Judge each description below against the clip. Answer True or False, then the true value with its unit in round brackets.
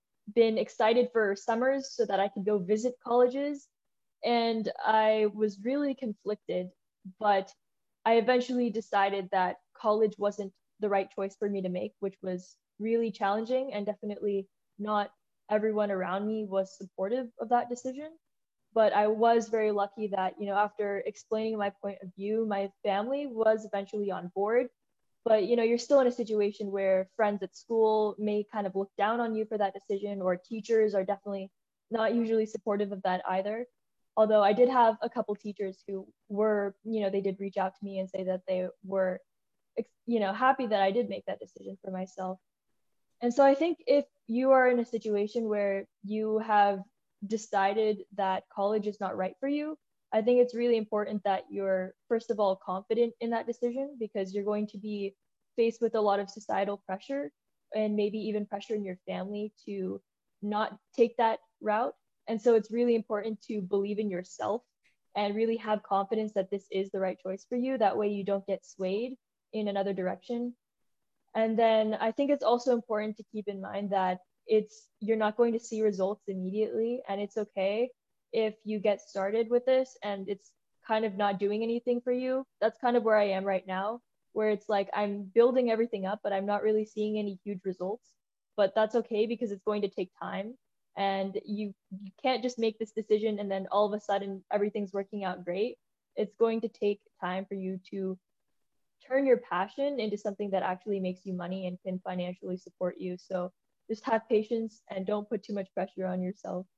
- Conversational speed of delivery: True (190 wpm)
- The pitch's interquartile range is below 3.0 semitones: True (2.5 semitones)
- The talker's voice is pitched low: False (210 Hz)